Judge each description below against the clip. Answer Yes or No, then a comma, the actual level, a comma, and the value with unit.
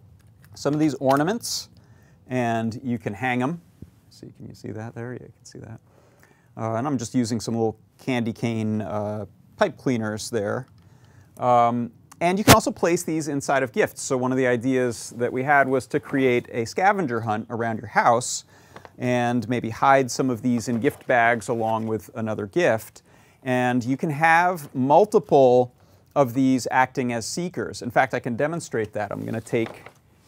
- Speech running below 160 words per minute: No, average, 185 wpm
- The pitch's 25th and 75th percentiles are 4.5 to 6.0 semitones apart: No, average, 3.0 semitones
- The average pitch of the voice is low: Yes, low, 125 Hz